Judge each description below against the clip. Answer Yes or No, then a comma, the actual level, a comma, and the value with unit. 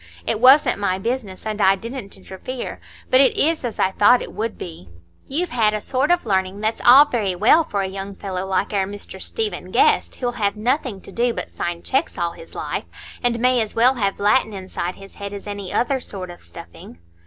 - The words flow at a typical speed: No, fast, 215 wpm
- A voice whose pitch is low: No, high, 210 Hz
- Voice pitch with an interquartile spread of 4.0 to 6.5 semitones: Yes, average, 4.5 semitones